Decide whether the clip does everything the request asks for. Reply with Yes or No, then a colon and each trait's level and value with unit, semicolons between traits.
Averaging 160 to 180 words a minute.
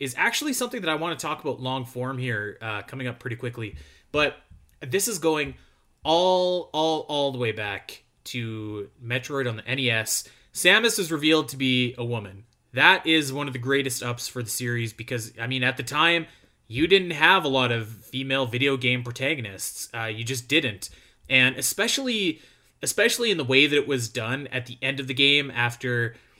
No: average, 195 wpm